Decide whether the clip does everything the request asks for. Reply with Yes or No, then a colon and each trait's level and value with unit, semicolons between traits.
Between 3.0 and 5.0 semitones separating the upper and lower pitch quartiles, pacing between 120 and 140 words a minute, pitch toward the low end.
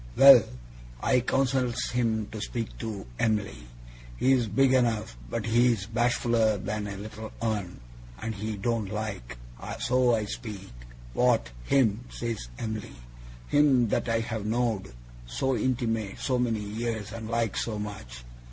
No: narrow, 2.5 semitones; slow, 135 wpm; low, 110 Hz